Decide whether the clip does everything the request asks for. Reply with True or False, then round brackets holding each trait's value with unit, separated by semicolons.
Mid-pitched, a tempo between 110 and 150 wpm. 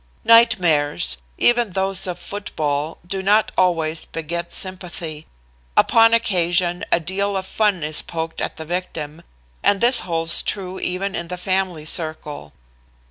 True (180 Hz; 135 wpm)